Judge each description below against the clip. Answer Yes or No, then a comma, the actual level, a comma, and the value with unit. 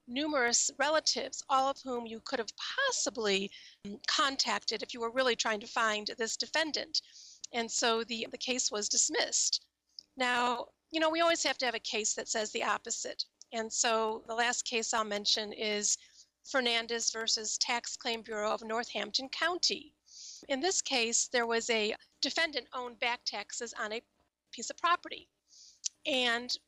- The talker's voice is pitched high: Yes, high, 235 Hz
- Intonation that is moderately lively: Yes, average, 3.0 semitones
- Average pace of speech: Yes, average, 160 wpm